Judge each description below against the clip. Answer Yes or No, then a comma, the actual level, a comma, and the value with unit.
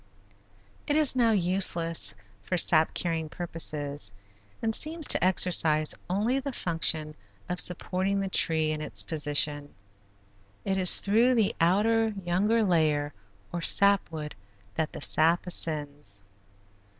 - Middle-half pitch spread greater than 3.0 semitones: Yes, average, 4.5 semitones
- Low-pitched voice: No, medium, 175 Hz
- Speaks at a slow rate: Yes, slow, 125 wpm